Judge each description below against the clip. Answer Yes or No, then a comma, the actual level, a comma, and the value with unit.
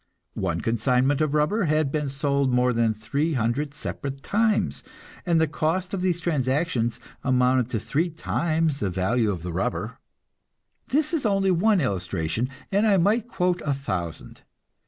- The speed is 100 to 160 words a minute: Yes, average, 155 wpm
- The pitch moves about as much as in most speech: No, wide, 6.4 semitones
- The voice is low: No, medium, 145 Hz